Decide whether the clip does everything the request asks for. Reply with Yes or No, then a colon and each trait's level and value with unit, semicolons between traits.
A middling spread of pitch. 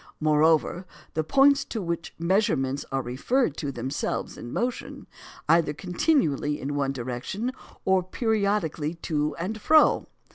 No: wide, 6.5 semitones